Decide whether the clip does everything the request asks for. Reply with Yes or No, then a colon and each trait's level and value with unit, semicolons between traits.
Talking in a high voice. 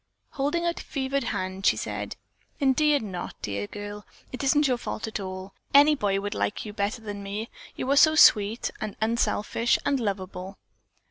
Yes: high, 220 Hz